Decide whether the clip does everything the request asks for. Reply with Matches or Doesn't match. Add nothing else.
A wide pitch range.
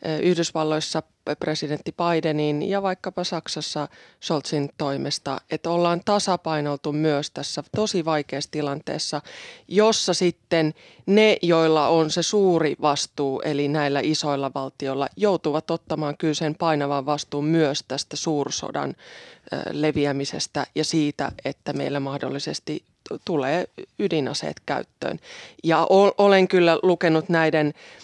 Doesn't match